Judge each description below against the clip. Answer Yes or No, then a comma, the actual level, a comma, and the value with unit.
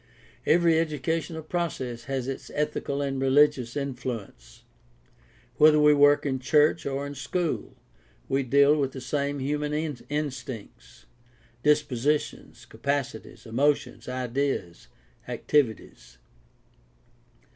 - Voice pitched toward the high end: No, medium, 140 Hz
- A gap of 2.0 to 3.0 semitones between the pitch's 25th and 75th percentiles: Yes, narrow, 2.4 semitones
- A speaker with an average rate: No, slow, 100 wpm